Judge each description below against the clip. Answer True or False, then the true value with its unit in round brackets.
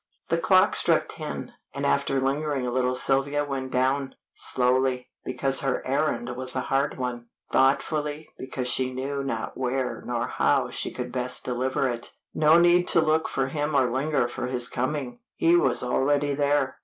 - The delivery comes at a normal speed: True (170 wpm)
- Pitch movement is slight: True (2.2 semitones)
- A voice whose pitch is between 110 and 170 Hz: True (135 Hz)